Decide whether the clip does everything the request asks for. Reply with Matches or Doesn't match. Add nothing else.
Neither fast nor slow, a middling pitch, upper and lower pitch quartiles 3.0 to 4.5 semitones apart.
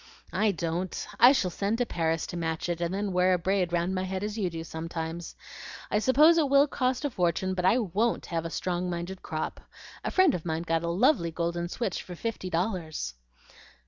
Doesn't match